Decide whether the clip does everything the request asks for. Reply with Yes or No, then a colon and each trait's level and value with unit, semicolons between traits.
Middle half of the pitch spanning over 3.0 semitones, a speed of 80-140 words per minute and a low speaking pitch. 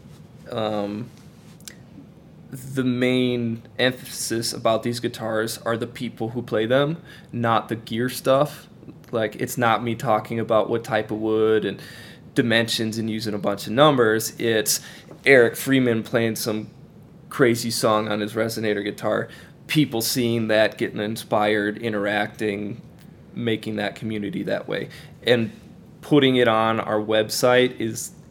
No: average, 2.7 semitones; slow, 135 wpm; low, 115 Hz